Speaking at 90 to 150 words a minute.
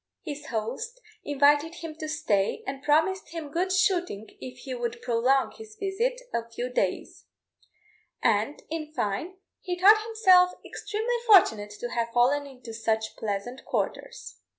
Yes: average, 145 wpm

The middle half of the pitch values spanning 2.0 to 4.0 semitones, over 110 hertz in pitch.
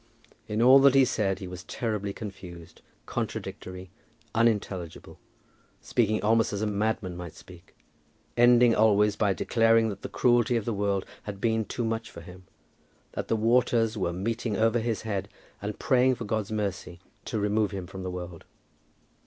No: average, 3.0 semitones; low, 105 Hz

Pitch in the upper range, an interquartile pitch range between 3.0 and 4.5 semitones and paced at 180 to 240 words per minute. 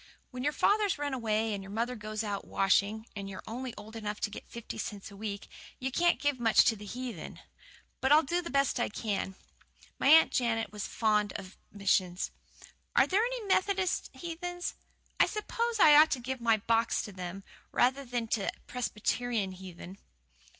No: high, 230 Hz; wide, 5.5 semitones; average, 185 wpm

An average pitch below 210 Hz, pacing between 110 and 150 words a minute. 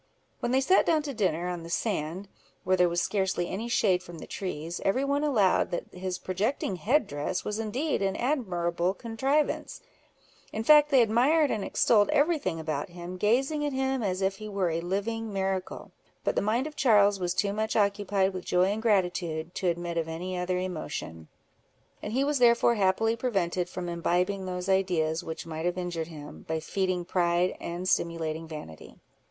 No: high, 190 Hz; average, 185 wpm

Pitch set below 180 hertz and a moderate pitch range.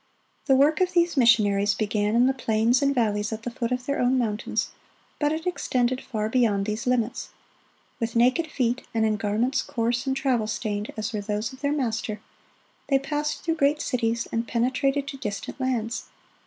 No: high, 240 Hz; average, 3.8 semitones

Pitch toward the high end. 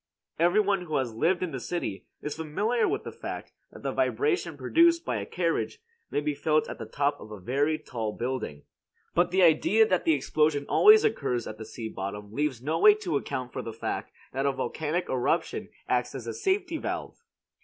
No: medium, 150 Hz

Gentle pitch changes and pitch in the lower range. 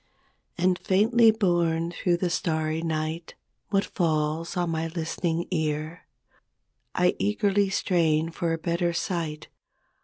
No: narrow, 2.2 semitones; medium, 170 Hz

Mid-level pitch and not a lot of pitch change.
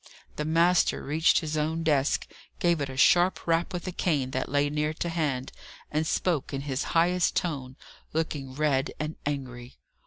No: medium, 150 Hz; average, 3.3 semitones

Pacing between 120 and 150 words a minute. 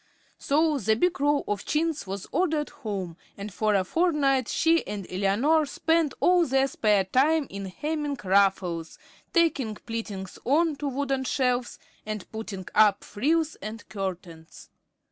Yes: average, 145 wpm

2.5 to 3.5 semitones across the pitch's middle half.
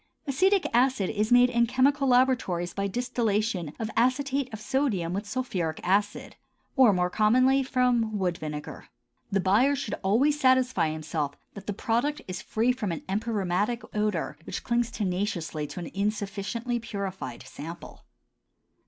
No: average, 5.2 semitones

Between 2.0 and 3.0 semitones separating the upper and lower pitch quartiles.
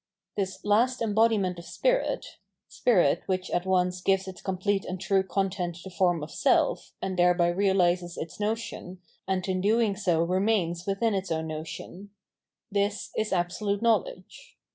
Yes: narrow, 2.5 semitones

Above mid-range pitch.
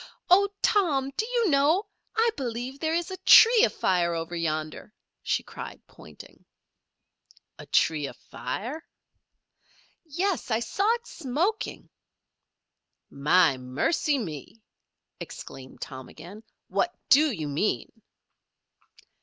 Yes: very high, 260 Hz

